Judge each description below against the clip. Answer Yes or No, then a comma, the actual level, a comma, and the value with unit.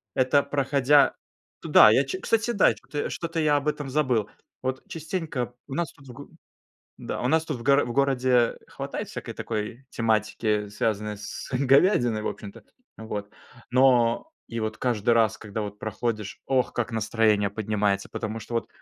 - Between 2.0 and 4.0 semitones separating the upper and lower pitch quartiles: No, average, 4.4 semitones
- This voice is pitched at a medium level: No, low, 120 Hz